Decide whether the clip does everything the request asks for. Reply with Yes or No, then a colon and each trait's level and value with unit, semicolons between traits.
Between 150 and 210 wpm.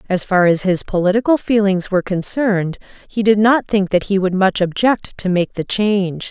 Yes: average, 200 wpm